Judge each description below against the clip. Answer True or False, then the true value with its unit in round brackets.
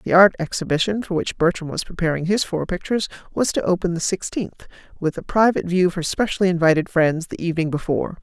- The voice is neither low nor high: True (175 Hz)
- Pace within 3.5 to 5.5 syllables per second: False (6.4 syllables/s)